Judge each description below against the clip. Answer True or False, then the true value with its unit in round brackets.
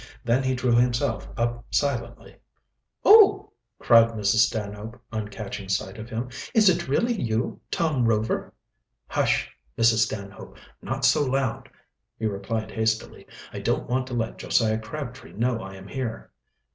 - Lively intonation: False (2.8 semitones)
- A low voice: True (115 Hz)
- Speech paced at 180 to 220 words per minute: False (145 wpm)